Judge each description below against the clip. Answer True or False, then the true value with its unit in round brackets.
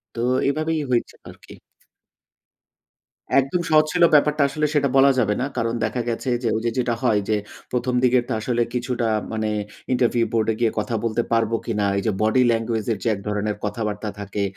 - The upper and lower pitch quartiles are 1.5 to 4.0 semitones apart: True (2.8 semitones)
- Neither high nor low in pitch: False (115 Hz)